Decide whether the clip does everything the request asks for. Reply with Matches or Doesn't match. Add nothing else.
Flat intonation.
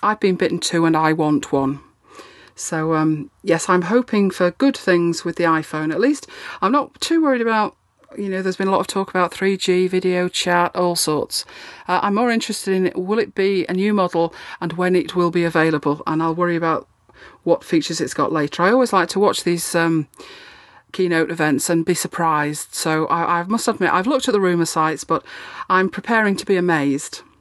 Doesn't match